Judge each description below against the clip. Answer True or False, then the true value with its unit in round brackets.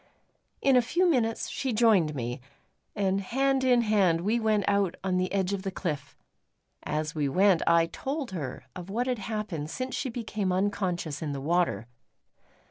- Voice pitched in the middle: False (195 Hz)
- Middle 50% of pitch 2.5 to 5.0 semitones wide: False (5.5 semitones)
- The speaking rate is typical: True (175 wpm)